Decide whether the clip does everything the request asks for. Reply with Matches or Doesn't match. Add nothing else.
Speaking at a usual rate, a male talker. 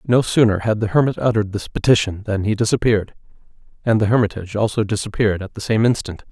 Matches